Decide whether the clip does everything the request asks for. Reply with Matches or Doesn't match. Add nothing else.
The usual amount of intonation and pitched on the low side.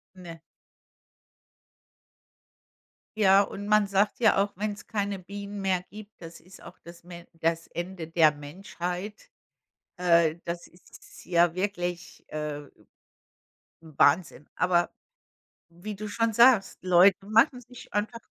Doesn't match